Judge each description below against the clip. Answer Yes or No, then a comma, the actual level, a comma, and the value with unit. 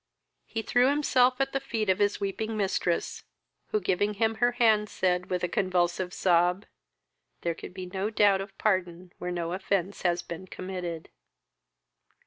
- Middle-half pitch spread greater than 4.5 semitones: No, average, 3.3 semitones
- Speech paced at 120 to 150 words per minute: No, average, 160 wpm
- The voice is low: No, high, 190 Hz